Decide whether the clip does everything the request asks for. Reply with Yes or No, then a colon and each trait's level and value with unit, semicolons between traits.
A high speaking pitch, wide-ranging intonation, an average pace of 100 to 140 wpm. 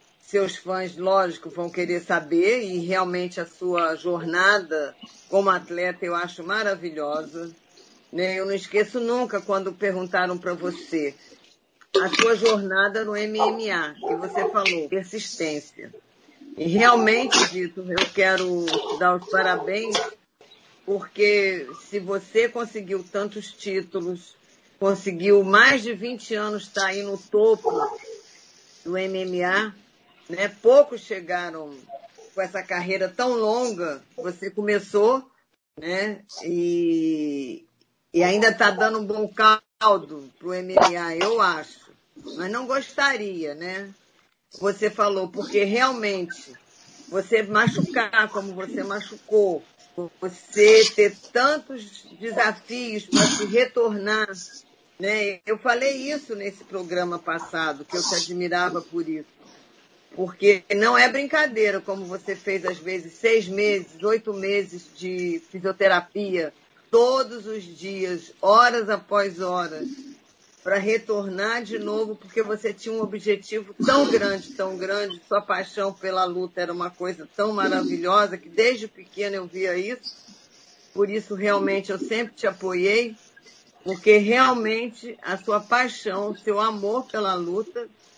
No: high, 200 Hz; average, 3.4 semitones; average, 125 wpm